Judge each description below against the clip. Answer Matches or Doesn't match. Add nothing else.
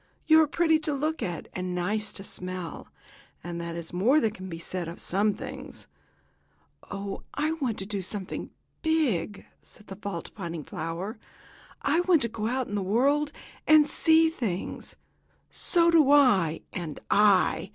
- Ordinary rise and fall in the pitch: Doesn't match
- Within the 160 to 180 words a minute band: Matches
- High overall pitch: Matches